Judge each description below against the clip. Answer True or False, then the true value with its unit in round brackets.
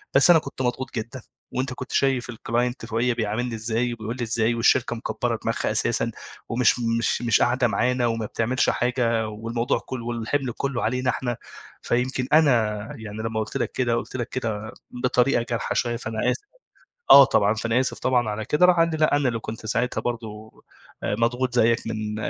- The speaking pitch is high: False (120 Hz)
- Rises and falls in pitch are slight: True (2.1 semitones)